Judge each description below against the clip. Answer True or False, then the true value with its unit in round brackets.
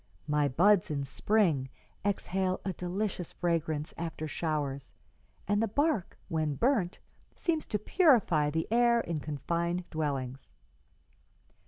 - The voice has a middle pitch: True (170 Hz)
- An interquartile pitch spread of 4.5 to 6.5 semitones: True (5.5 semitones)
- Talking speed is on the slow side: True (120 wpm)